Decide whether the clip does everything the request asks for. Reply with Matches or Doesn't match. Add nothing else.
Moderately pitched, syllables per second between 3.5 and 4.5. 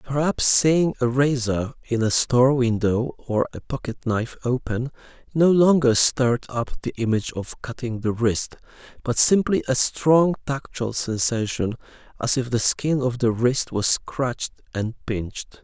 Doesn't match